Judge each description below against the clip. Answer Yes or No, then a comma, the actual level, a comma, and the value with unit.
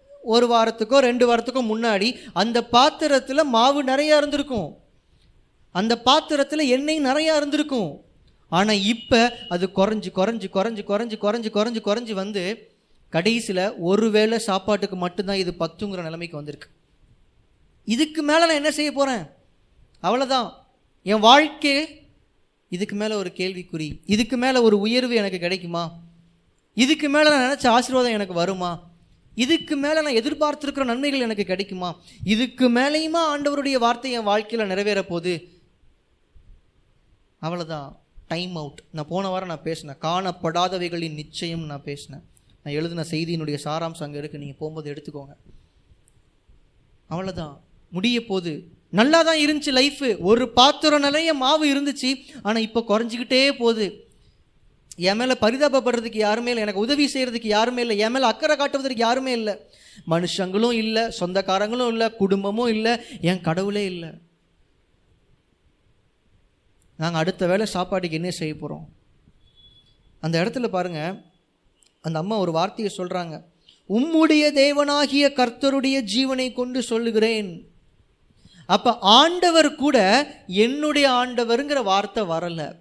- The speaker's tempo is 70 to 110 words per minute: No, average, 120 wpm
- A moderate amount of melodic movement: No, wide, 6.4 semitones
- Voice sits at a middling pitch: No, high, 220 Hz